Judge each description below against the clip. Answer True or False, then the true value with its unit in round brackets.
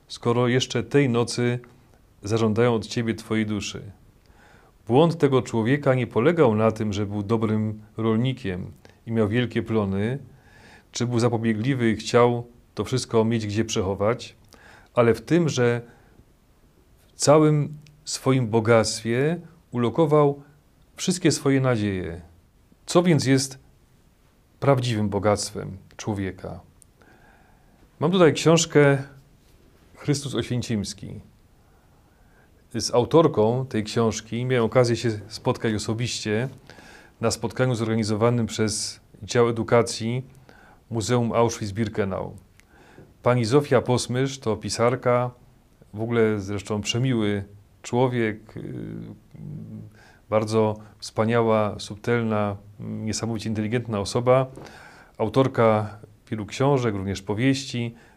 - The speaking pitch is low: True (115 Hz)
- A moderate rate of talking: False (100 wpm)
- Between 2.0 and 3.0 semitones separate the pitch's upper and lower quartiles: True (2.7 semitones)